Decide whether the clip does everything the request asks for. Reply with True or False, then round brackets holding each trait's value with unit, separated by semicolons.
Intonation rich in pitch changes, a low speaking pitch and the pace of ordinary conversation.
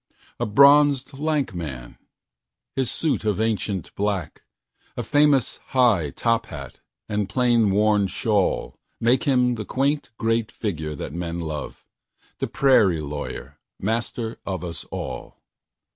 False (6.2 semitones; 110 Hz; 115 wpm)